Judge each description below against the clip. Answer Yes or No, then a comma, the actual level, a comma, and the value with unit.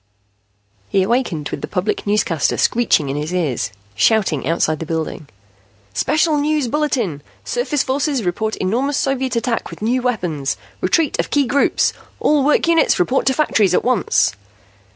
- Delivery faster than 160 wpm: No, average, 150 wpm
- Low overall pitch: No, high, 230 Hz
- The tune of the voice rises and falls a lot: Yes, wide, 8.4 semitones